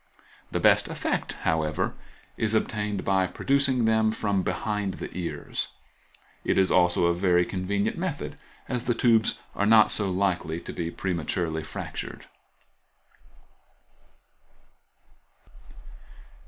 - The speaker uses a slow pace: Yes, slow, 115 wpm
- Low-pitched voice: Yes, low, 100 Hz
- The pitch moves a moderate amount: Yes, average, 4.0 semitones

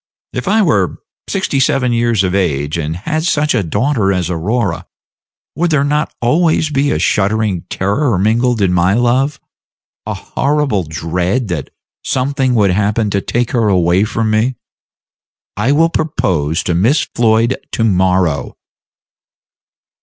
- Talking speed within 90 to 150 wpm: Yes, average, 145 wpm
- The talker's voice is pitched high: No, low, 110 Hz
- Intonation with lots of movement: Yes, wide, 6.5 semitones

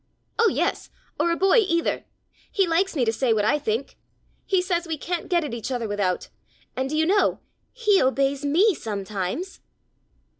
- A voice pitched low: No, very high, 305 Hz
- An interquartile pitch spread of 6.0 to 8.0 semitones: Yes, wide, 7.5 semitones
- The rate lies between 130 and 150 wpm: No, average, 180 wpm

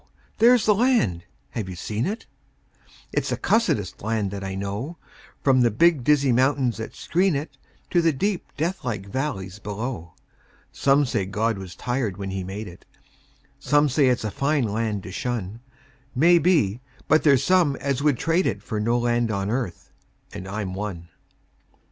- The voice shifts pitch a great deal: Yes, wide, 6.6 semitones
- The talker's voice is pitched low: Yes, low, 120 Hz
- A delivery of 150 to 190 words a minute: Yes, average, 165 wpm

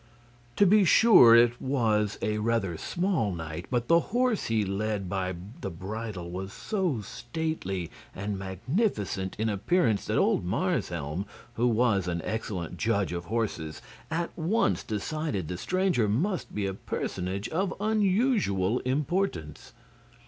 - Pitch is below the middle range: Yes, low, 110 Hz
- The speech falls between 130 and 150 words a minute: Yes, slow, 135 wpm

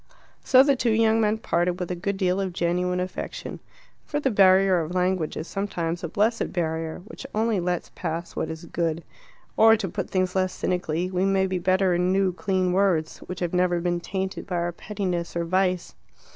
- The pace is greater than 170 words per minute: Yes, average, 200 wpm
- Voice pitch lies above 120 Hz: Yes, medium, 185 Hz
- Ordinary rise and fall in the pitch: No, narrow, 2.1 semitones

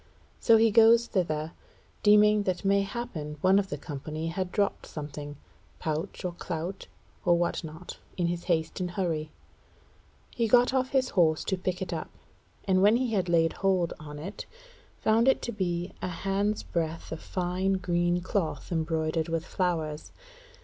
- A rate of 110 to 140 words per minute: No, average, 165 wpm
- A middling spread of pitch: Yes, average, 3.7 semitones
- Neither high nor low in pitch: Yes, medium, 180 Hz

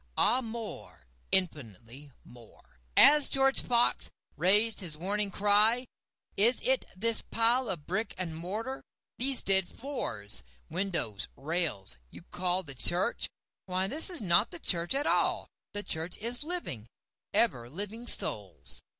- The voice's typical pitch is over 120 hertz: Yes, high, 190 Hz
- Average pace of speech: No, slow, 115 wpm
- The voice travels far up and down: Yes, wide, 7.4 semitones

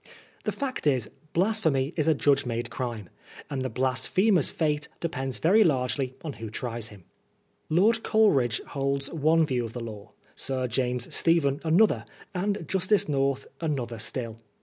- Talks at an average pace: Yes, average, 165 wpm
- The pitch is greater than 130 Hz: Yes, medium, 140 Hz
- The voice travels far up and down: No, average, 4.9 semitones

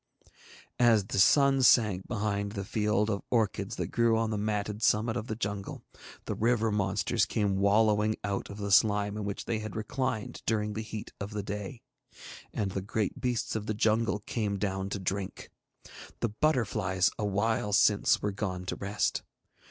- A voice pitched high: No, low, 105 Hz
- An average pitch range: No, narrow, 1.8 semitones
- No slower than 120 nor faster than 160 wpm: No, average, 175 wpm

